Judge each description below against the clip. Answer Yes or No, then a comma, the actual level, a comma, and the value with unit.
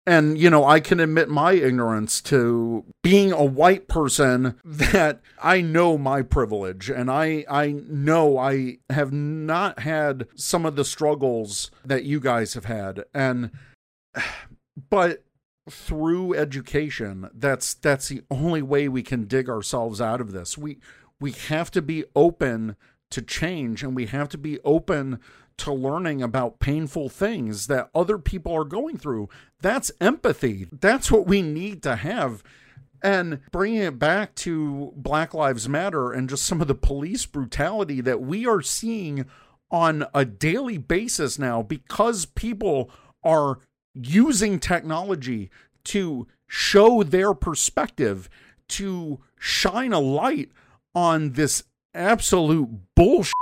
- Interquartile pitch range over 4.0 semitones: Yes, average, 4.8 semitones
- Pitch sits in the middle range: Yes, medium, 145 Hz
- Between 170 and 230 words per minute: No, average, 140 wpm